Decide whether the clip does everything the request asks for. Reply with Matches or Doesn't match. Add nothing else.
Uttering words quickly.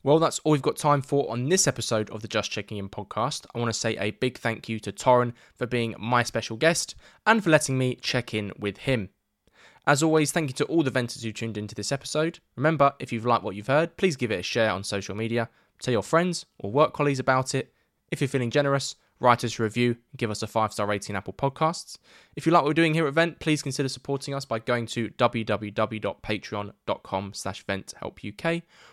Matches